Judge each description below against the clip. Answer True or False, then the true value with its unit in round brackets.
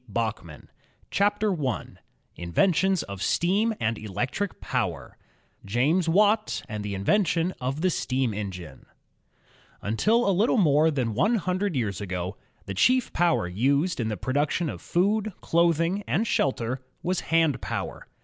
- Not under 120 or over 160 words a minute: True (150 wpm)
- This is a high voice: False (155 Hz)